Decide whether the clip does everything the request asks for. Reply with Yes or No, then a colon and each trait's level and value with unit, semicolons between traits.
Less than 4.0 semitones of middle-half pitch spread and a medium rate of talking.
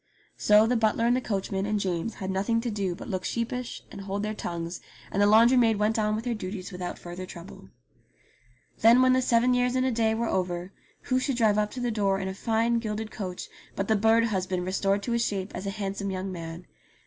No: average, 3.4 semitones; fast, 230 wpm